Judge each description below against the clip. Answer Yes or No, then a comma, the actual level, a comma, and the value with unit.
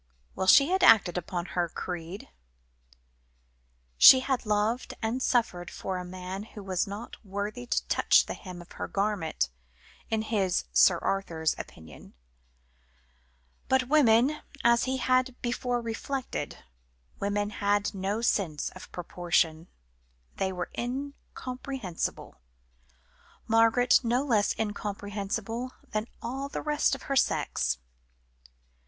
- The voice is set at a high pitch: Yes, high, 210 Hz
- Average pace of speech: No, slow, 125 wpm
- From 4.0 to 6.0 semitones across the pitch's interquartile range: Yes, average, 4.9 semitones